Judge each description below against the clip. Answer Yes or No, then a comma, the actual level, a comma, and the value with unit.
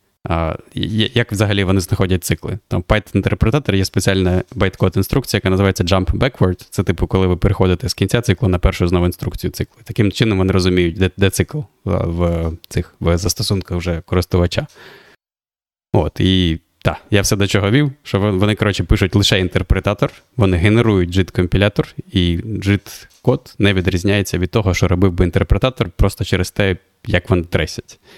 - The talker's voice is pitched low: Yes, very low, 95 Hz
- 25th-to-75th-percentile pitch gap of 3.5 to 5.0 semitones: No, average, 3.0 semitones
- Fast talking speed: Yes, fast, 165 wpm